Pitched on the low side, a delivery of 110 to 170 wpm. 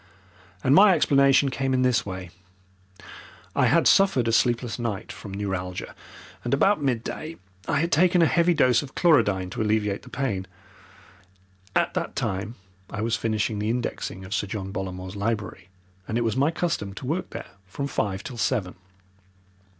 Yes: low, 115 Hz; average, 165 wpm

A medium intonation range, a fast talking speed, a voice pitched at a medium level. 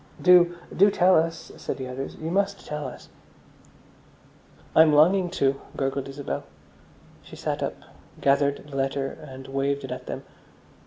No: average, 4.2 semitones; average, 150 wpm; medium, 145 Hz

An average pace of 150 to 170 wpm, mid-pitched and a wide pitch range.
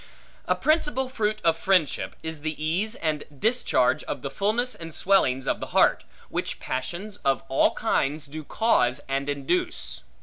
Yes: average, 160 wpm; medium, 160 Hz; wide, 7.3 semitones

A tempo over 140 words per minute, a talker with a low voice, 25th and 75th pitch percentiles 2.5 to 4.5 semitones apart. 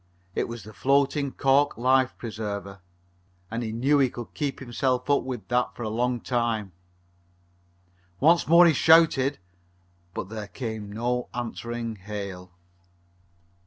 No: slow, 135 wpm; low, 120 Hz; average, 3.6 semitones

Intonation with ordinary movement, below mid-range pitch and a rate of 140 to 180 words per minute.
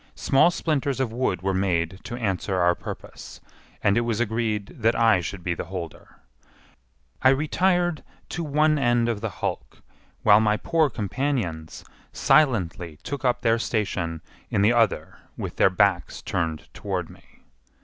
No: wide, 6.2 semitones; low, 110 Hz; average, 155 wpm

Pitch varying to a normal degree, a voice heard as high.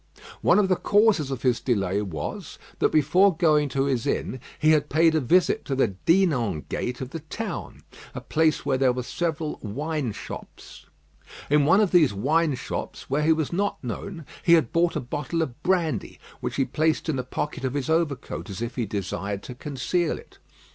No: average, 4.7 semitones; medium, 150 Hz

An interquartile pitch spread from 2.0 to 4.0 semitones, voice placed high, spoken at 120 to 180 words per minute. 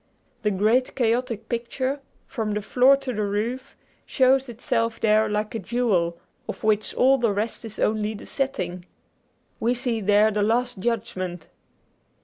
Yes: average, 3.0 semitones; high, 225 Hz; average, 150 wpm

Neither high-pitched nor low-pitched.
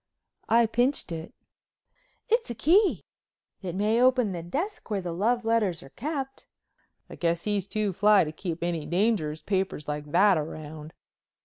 No: high, 200 Hz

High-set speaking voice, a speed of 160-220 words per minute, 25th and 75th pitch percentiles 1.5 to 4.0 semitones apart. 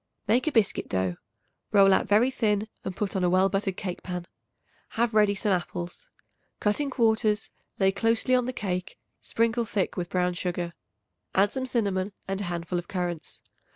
Yes: high, 200 Hz; average, 180 wpm; average, 3.7 semitones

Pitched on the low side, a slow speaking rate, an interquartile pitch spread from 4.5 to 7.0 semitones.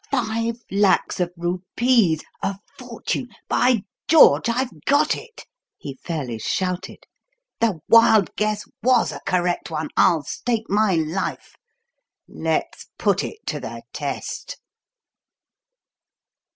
No: high, 210 Hz; slow, 110 wpm; wide, 5.5 semitones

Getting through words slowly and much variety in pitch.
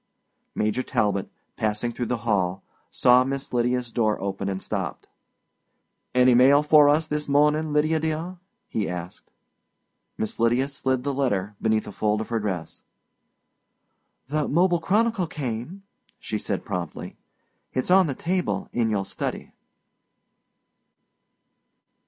Yes: slow, 130 wpm; wide, 5.8 semitones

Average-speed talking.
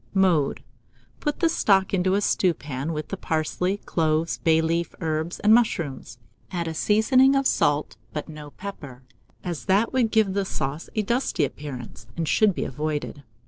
Yes: average, 165 wpm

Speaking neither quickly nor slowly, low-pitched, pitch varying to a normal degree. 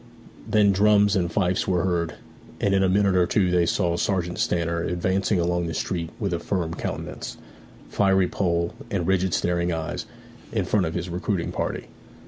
No: average, 175 wpm; very low, 90 Hz; narrow, 2.1 semitones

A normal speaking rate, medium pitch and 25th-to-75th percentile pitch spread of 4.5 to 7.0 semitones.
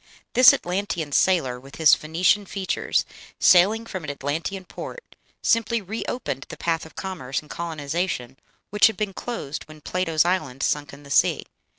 Yes: average, 165 wpm; medium, 170 Hz; average, 5.2 semitones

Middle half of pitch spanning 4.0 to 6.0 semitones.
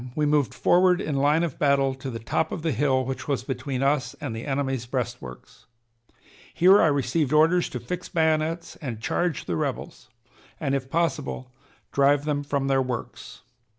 No: average, 3.1 semitones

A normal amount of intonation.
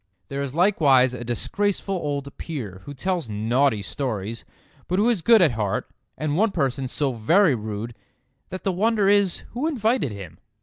No: wide, 8.6 semitones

